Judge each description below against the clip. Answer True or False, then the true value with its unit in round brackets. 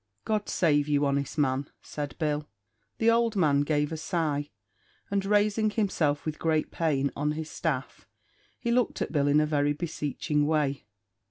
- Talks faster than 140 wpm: True (165 wpm)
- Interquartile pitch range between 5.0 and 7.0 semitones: False (3.4 semitones)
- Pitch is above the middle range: False (150 Hz)